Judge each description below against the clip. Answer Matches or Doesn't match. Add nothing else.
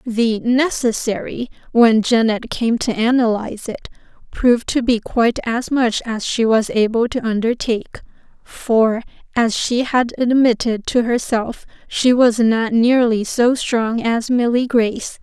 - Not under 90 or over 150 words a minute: Matches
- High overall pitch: Matches